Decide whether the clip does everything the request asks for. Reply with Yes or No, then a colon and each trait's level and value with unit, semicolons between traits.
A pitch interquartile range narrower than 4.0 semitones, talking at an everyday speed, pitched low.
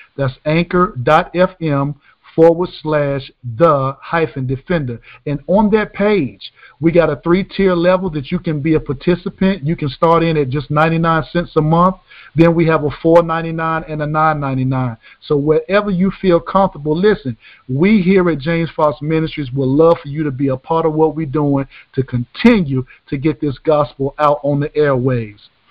No: average, 3.3 semitones; average, 175 wpm; medium, 155 Hz